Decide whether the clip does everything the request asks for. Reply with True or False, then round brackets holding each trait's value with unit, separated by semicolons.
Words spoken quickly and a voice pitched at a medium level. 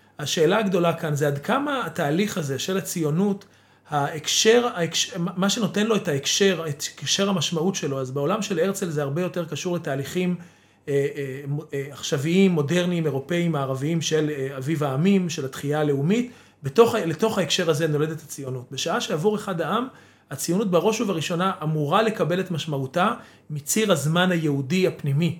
True (155 wpm; 165 Hz)